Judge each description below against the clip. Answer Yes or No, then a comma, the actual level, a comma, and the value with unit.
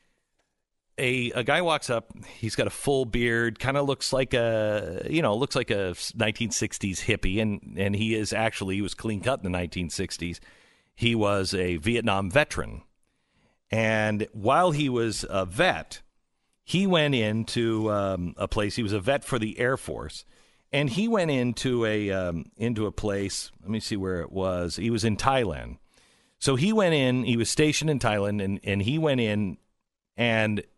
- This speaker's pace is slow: No, average, 185 wpm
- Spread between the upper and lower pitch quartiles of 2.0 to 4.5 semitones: Yes, average, 4.2 semitones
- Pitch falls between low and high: No, low, 110 Hz